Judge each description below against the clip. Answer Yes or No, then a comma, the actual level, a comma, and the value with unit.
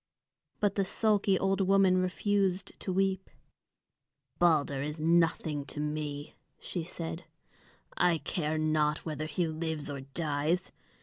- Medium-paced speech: No, slow, 125 wpm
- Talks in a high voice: No, medium, 165 Hz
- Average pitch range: Yes, average, 3.7 semitones